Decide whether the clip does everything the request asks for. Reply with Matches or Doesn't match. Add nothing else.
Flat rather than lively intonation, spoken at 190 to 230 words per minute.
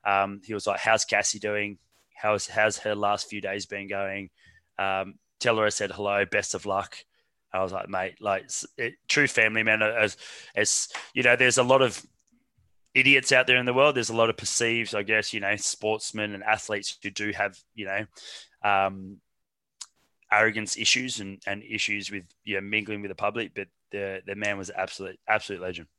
Matches